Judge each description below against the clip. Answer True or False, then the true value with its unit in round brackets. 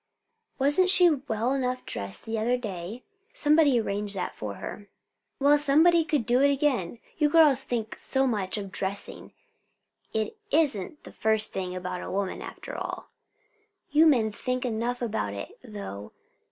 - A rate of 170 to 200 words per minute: False (155 wpm)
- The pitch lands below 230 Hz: False (240 Hz)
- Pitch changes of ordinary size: False (6.0 semitones)